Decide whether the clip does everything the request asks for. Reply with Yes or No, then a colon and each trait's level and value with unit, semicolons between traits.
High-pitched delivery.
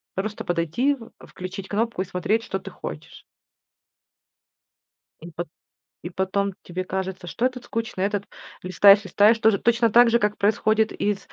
Yes: high, 200 Hz